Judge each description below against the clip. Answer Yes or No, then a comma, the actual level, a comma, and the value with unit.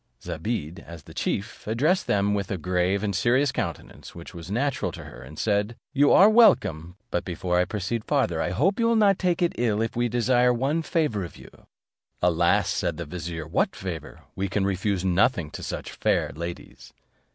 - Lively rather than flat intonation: Yes, wide, 6.7 semitones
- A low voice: Yes, low, 105 Hz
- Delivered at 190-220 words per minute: Yes, average, 195 wpm